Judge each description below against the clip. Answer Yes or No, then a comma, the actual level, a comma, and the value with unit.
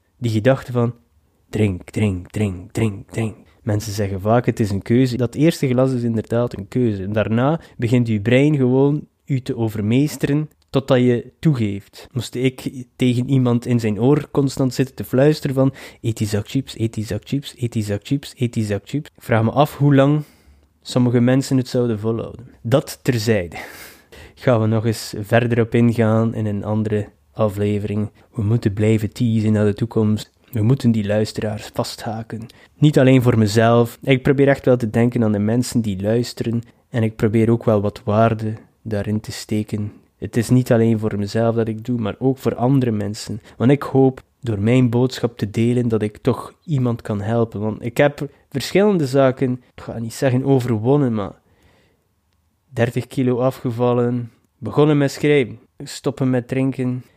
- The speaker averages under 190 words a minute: Yes, average, 180 wpm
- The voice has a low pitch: Yes, low, 120 Hz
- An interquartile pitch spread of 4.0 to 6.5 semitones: No, average, 3.3 semitones